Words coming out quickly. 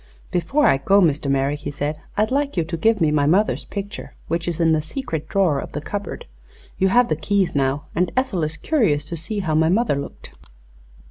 Yes: fast, 215 wpm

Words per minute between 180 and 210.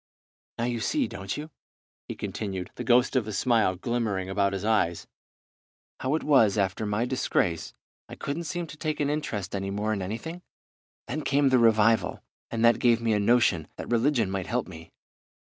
Yes: average, 190 wpm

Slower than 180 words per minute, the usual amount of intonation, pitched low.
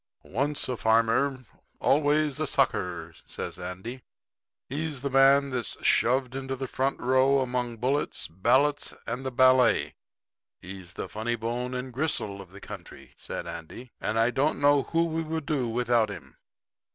Yes: average, 155 wpm; average, 3.4 semitones; low, 130 Hz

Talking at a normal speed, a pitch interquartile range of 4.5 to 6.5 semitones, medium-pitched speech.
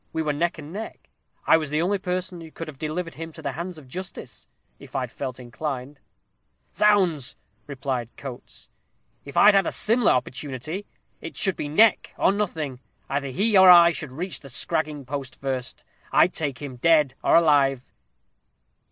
Yes: average, 175 wpm; average, 4.8 semitones; medium, 155 Hz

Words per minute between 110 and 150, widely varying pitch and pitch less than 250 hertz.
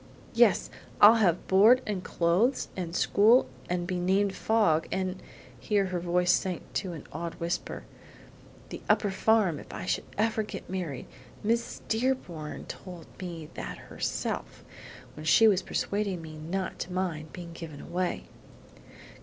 No: average, 145 wpm; average, 3.4 semitones; medium, 185 Hz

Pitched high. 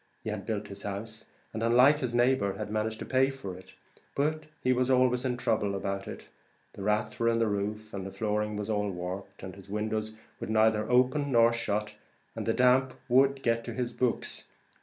No: low, 110 Hz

